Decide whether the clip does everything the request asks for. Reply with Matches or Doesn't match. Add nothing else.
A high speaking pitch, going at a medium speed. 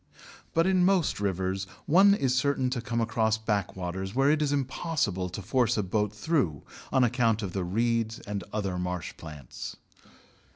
Doesn't match